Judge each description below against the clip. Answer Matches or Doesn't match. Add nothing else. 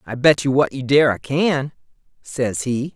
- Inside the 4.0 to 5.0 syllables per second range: Matches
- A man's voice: Matches